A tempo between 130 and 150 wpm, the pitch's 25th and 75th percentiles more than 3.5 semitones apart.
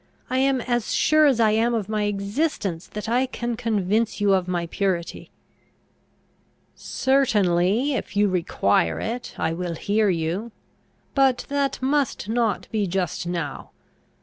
Yes: average, 145 wpm; average, 5.2 semitones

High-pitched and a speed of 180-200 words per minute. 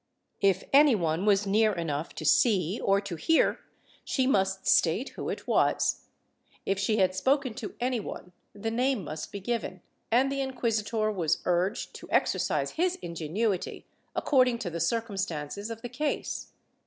No: high, 205 Hz; average, 160 wpm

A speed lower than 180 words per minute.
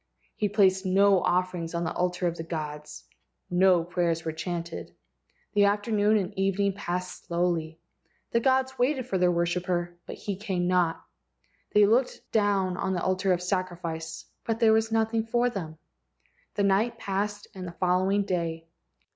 Yes: average, 165 wpm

